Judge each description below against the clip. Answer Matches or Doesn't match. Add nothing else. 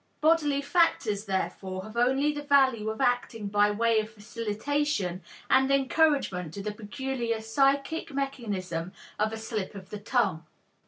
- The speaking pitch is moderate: Doesn't match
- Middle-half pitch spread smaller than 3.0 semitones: Doesn't match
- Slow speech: Doesn't match